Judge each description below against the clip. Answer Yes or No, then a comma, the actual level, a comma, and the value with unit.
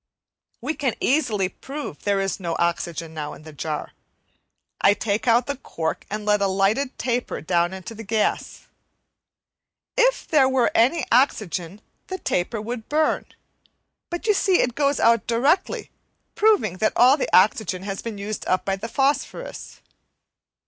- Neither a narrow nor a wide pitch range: No, wide, 6.1 semitones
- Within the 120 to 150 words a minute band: No, average, 160 wpm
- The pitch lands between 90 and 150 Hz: No, high, 220 Hz